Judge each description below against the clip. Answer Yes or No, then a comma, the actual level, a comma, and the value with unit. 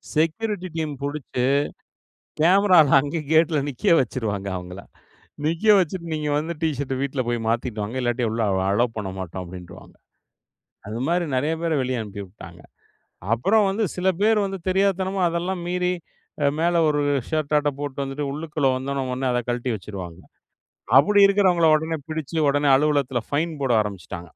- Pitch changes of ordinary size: No, wide, 5.8 semitones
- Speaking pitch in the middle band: Yes, medium, 145 Hz